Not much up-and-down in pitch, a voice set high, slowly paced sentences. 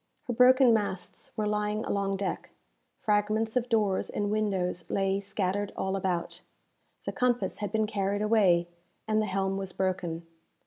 No: narrow, 2.0 semitones; high, 205 Hz; average, 150 wpm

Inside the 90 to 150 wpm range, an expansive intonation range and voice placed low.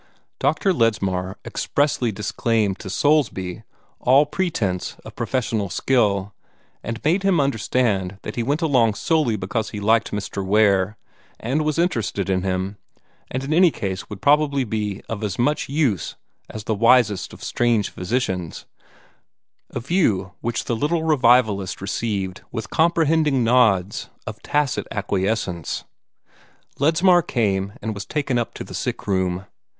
Yes: average, 140 wpm; wide, 6.1 semitones; low, 115 Hz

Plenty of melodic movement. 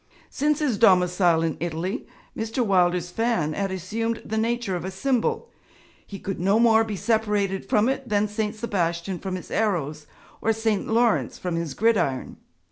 No: average, 3.9 semitones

